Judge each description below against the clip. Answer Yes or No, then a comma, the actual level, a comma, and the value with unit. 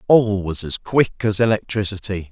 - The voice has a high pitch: No, low, 105 Hz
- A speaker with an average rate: Yes, average, 155 wpm